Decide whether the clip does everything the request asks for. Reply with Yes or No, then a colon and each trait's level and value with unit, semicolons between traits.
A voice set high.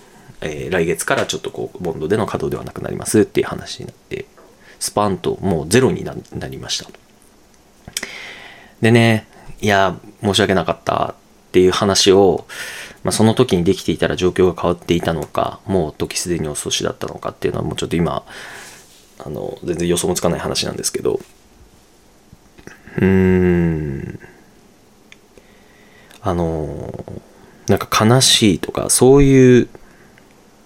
No: very low, 95 Hz